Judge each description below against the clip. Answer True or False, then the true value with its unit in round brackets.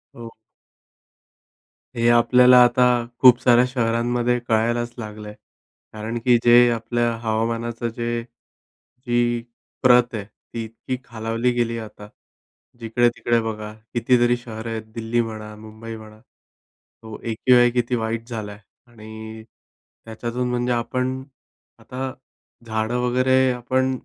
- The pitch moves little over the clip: True (1.5 semitones)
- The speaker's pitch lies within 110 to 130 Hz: True (120 Hz)